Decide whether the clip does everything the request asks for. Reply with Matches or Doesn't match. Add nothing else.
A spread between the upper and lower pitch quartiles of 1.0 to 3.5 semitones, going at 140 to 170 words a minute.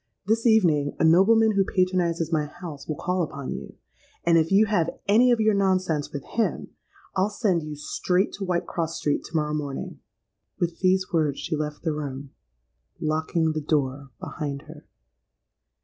Doesn't match